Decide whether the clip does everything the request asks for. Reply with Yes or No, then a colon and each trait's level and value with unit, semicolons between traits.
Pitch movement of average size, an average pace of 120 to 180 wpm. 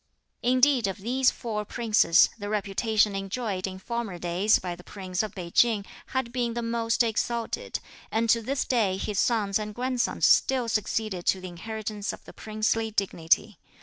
Yes: average, 3.2 semitones; average, 170 wpm